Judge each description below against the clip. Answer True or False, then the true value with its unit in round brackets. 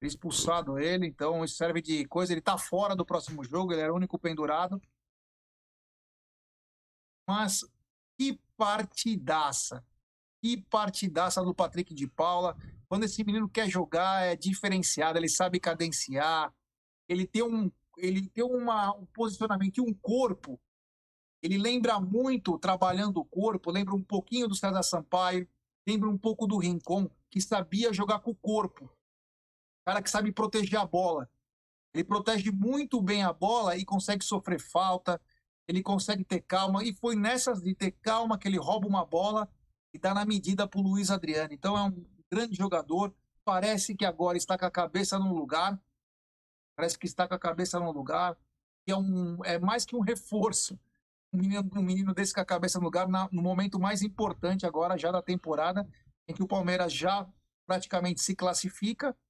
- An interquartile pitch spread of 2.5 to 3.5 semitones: True (3.0 semitones)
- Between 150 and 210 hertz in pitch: True (190 Hz)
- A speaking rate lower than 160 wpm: False (170 wpm)